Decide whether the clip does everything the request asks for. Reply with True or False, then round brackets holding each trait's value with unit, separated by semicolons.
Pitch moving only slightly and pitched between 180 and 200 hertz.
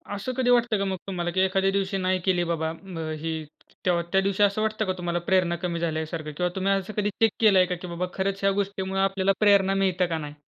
True (2.2 semitones; 190 Hz)